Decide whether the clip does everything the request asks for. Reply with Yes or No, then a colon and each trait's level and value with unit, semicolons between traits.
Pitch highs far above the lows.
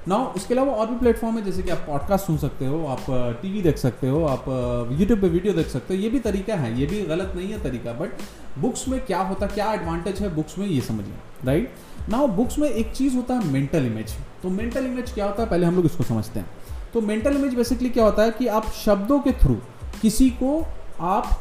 Yes: wide, 8.1 semitones